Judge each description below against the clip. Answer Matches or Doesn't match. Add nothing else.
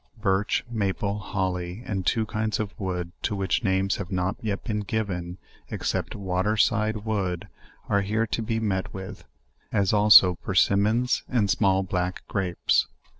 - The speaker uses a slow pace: Doesn't match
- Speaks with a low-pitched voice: Matches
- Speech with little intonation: Matches